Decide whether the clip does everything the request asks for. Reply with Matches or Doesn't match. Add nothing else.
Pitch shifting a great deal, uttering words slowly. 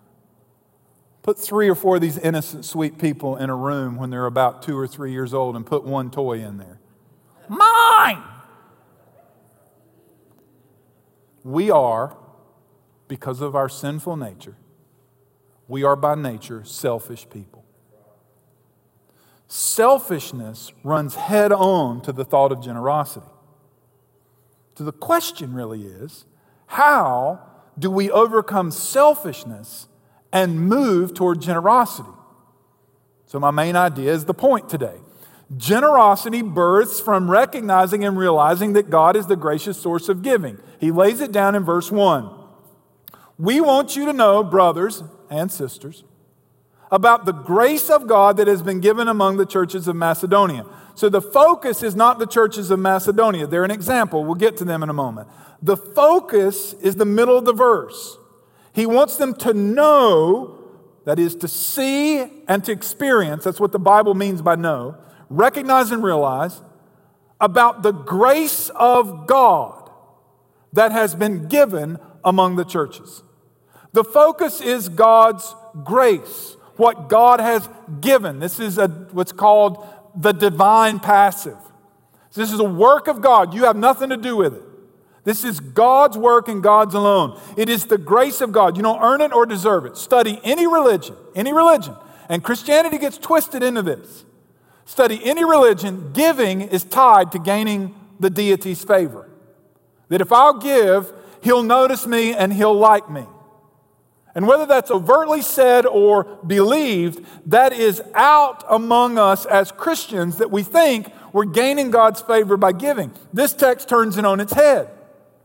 Doesn't match